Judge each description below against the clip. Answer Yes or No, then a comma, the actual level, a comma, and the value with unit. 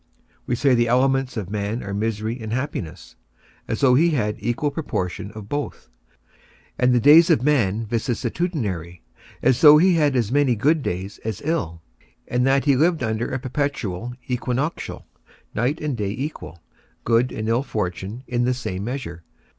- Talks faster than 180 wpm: No, average, 170 wpm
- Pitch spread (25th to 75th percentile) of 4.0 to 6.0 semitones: Yes, average, 4.9 semitones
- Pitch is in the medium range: No, low, 120 Hz